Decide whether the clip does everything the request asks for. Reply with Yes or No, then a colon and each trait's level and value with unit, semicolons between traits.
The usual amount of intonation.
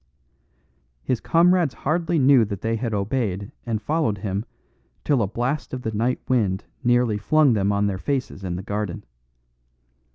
Yes: average, 4.8 semitones